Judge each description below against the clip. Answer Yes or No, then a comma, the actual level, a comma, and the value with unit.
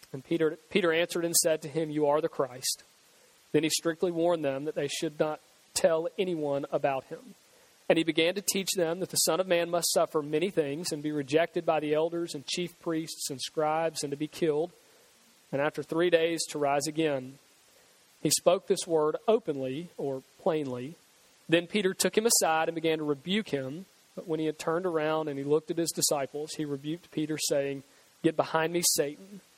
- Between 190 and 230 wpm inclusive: Yes, average, 200 wpm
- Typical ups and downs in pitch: No, narrow, 2.3 semitones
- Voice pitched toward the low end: No, medium, 160 Hz